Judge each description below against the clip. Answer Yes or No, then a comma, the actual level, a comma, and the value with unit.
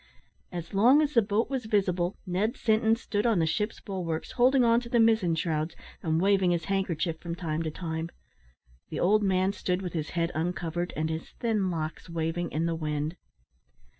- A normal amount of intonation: Yes, average, 4.4 semitones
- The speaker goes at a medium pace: Yes, average, 190 wpm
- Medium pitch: Yes, medium, 180 Hz